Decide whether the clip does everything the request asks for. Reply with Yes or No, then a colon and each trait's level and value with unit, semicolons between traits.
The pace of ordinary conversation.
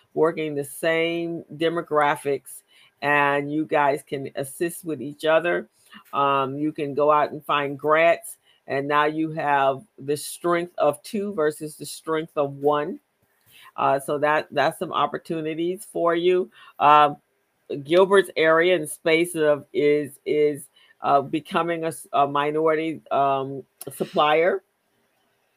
No: slow, 130 wpm